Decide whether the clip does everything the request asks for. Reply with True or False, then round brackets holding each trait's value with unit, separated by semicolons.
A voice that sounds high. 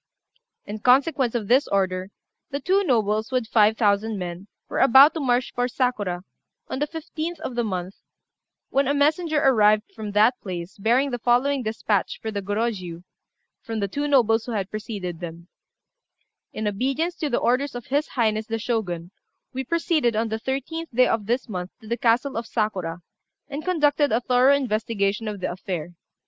True (230 Hz)